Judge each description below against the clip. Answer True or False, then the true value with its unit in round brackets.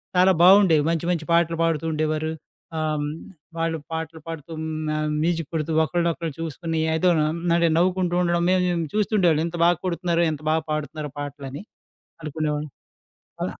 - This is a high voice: False (165 Hz)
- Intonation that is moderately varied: False (2.0 semitones)